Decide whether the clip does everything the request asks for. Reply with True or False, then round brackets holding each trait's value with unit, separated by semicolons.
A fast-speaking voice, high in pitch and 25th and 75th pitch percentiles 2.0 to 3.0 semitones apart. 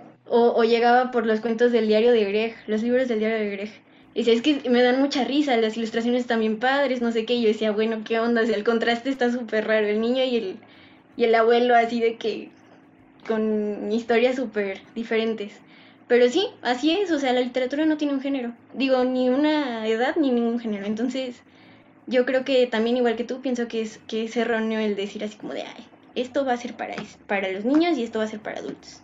True (230 wpm; 235 Hz; 2.6 semitones)